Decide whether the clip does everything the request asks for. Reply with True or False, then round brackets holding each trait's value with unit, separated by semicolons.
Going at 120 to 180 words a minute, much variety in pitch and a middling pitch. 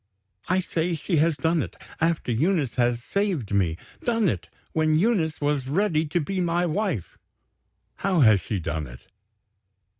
True (155 wpm; 6.8 semitones; 160 Hz)